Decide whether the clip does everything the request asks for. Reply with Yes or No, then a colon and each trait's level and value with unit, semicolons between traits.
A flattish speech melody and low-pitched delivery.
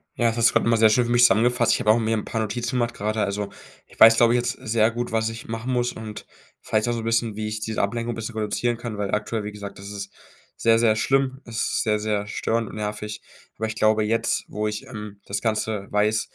Yes: narrow, 1.7 semitones; low, 110 Hz